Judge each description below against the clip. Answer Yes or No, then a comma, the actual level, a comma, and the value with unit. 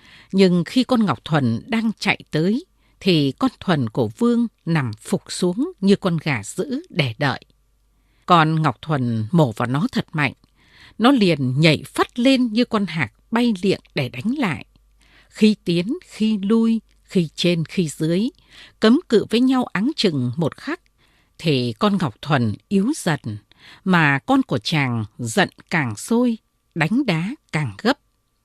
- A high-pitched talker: No, medium, 175 Hz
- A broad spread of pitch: Yes, wide, 8.0 semitones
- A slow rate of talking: Yes, slow, 160 wpm